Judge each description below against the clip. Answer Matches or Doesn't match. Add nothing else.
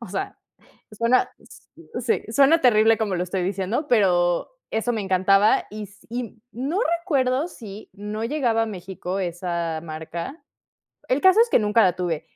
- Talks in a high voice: Matches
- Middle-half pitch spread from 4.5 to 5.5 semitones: Matches